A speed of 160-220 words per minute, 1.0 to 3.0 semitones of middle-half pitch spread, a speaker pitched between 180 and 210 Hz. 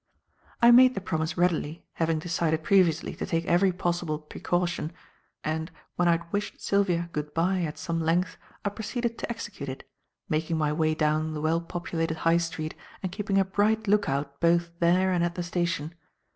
No: average, 185 wpm; average, 2.7 semitones; medium, 170 Hz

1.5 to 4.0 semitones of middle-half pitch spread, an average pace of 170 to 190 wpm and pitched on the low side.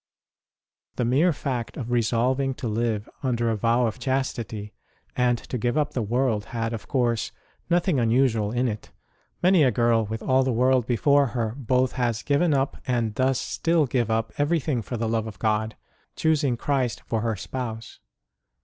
Yes: average, 2.8 semitones; average, 175 wpm; low, 120 Hz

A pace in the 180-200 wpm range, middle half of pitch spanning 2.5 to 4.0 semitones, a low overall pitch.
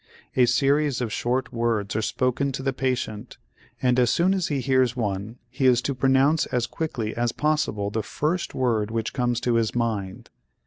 Yes: average, 185 wpm; average, 2.9 semitones; low, 125 Hz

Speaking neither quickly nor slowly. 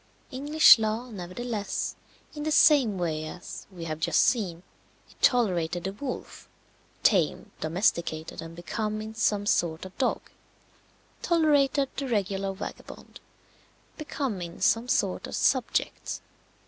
No: slow, 125 wpm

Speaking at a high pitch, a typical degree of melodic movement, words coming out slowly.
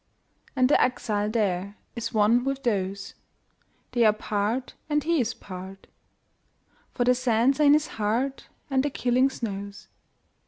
Yes: high, 235 Hz; average, 4.3 semitones; slow, 125 wpm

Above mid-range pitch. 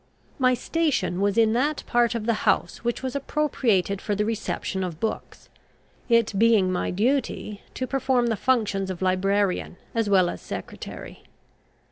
Yes: high, 225 Hz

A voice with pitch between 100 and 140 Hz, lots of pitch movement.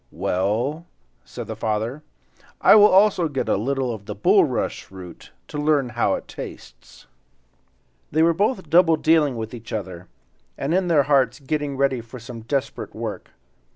Yes: low, 135 Hz; wide, 5.8 semitones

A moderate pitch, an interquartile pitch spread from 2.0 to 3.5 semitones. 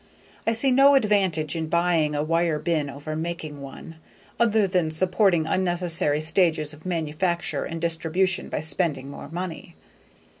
Yes: medium, 165 Hz; average, 3.0 semitones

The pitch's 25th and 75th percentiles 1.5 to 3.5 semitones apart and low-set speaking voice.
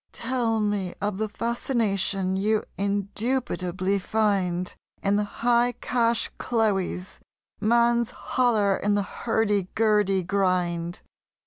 No: average, 3.1 semitones; high, 205 Hz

